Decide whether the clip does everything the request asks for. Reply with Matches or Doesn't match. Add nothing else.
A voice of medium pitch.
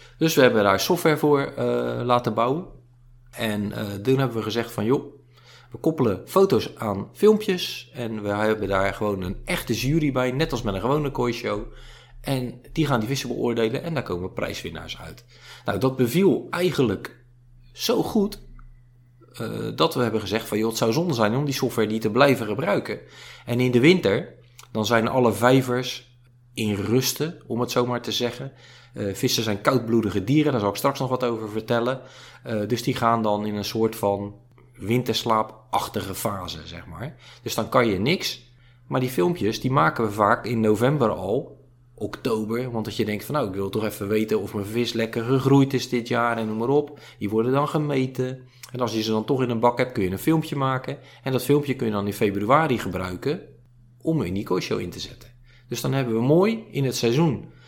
Doesn't match